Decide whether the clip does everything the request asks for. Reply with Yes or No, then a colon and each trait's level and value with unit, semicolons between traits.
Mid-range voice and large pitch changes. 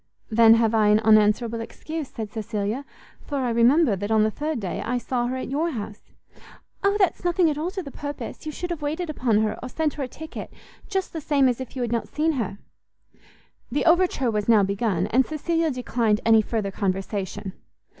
No: high, 245 Hz; wide, 6.1 semitones